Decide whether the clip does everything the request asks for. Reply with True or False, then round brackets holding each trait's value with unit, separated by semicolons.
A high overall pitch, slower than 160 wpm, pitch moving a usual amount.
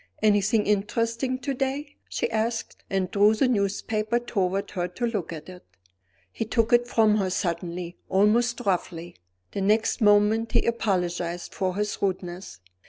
True (210 Hz; 150 wpm; 3.8 semitones)